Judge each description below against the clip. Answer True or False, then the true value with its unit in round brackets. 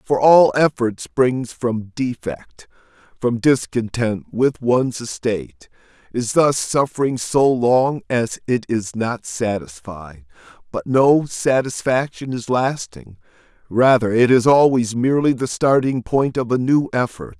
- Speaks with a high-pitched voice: False (125 Hz)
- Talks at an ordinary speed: False (125 wpm)